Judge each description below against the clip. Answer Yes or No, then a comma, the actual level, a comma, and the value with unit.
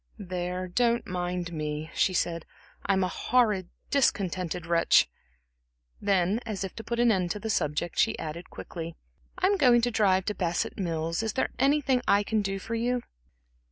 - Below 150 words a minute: No, average, 170 wpm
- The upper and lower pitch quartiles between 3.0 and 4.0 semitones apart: No, average, 4.8 semitones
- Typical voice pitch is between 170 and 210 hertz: Yes, high, 190 Hz